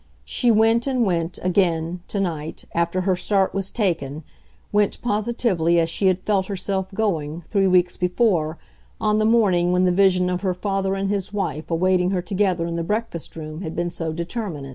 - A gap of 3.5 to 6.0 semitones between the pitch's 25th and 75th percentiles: No, average, 3.1 semitones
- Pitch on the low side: No, medium, 185 Hz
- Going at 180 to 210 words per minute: Yes, average, 185 wpm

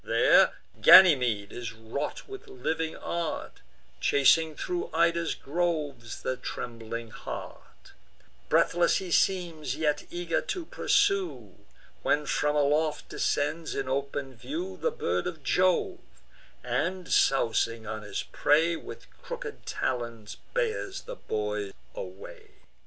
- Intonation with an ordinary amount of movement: No, wide, 6.7 semitones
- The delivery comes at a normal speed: No, slow, 115 wpm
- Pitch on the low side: No, medium, 150 Hz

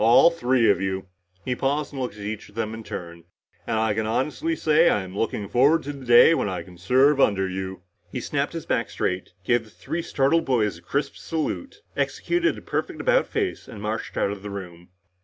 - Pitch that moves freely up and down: Yes, wide, 6.8 semitones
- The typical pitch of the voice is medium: No, low, 115 Hz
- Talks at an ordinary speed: No, fast, 215 wpm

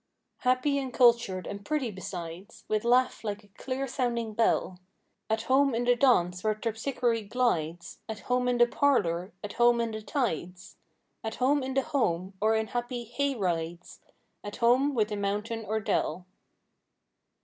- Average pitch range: Yes, average, 3.9 semitones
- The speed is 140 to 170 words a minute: Yes, average, 165 wpm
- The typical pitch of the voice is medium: No, high, 230 Hz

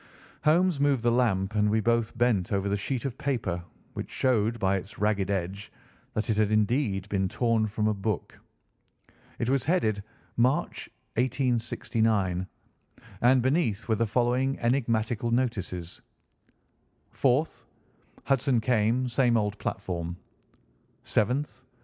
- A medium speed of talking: No, slow, 130 wpm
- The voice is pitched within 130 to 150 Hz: No, low, 115 Hz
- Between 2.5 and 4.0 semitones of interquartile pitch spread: Yes, average, 3.7 semitones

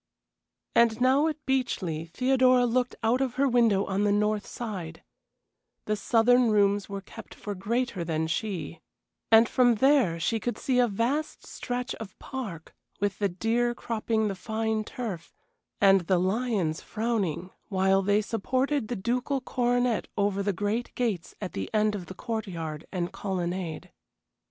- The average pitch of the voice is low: No, high, 215 Hz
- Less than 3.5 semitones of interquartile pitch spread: No, average, 4.2 semitones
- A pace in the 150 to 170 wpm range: Yes, average, 155 wpm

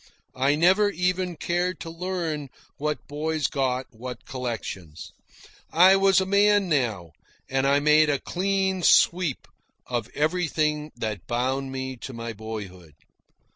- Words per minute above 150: No, slow, 135 wpm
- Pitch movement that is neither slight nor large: No, wide, 6.1 semitones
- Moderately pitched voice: Yes, medium, 150 Hz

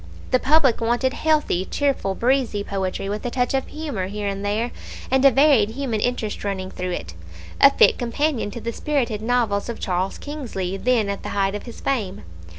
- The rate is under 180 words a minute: No, average, 190 wpm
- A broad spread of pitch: No, average, 4.9 semitones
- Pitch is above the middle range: Yes, high, 230 Hz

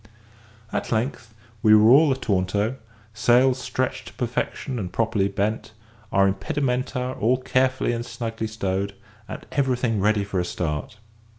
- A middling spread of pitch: Yes, average, 4.0 semitones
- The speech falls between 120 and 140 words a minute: Yes, slow, 135 wpm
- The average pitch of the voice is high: No, low, 115 Hz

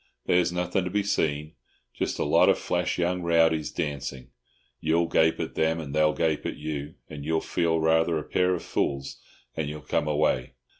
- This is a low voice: Yes, very low, 80 Hz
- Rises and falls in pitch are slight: Yes, narrow, 2.2 semitones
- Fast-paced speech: No, average, 185 wpm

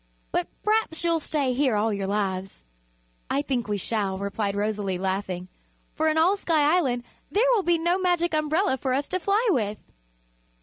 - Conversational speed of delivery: Yes, average, 175 wpm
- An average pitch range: No, wide, 8.8 semitones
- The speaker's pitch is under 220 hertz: No, very high, 265 Hz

